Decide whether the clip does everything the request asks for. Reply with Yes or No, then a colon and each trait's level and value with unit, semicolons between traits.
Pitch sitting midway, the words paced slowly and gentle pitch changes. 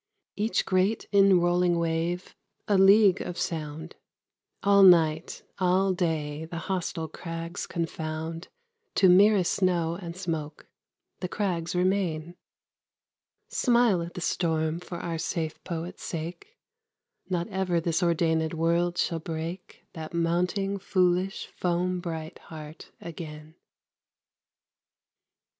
Yes: medium, 175 Hz; slow, 110 wpm; narrow, 2.2 semitones